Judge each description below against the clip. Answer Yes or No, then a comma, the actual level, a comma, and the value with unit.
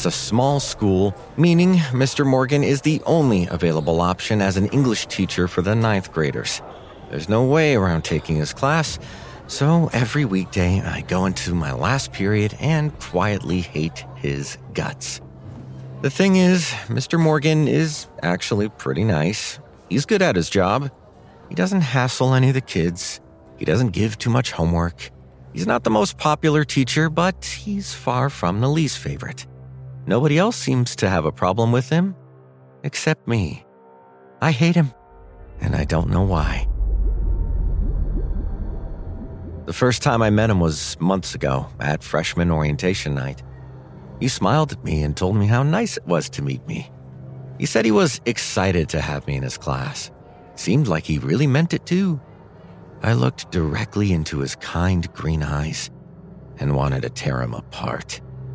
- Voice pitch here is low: Yes, very low, 95 Hz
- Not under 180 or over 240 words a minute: No, average, 165 wpm